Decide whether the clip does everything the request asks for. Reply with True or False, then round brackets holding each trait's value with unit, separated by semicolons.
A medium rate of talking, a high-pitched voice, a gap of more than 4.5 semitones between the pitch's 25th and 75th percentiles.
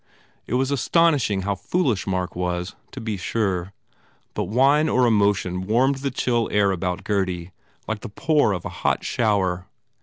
False (170 wpm; 105 Hz; 5.3 semitones)